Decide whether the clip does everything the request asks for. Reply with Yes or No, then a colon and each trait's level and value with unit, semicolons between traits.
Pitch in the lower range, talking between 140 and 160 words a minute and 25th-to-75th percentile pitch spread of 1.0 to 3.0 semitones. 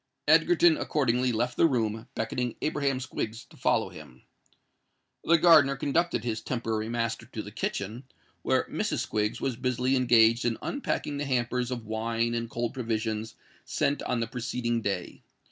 Yes: low, 120 Hz; average, 155 wpm; average, 2.7 semitones